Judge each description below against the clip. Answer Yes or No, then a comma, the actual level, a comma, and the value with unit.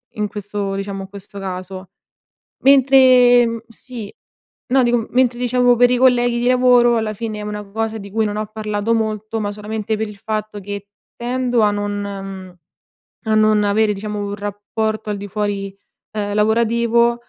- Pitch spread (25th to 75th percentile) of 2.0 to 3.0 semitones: Yes, narrow, 2.6 semitones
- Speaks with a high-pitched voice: Yes, high, 215 Hz